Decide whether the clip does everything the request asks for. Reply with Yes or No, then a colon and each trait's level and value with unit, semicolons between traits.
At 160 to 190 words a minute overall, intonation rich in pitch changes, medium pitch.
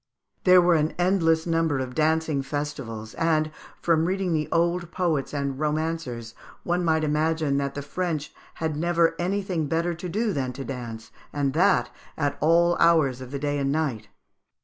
No: average, 170 wpm; average, 3.3 semitones; medium, 160 Hz